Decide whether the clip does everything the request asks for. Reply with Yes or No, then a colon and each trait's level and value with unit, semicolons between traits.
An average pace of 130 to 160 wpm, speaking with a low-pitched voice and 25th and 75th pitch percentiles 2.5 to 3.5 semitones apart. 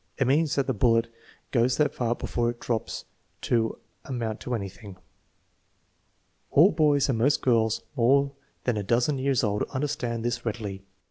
Yes: average, 155 wpm; low, 120 Hz; average, 3.2 semitones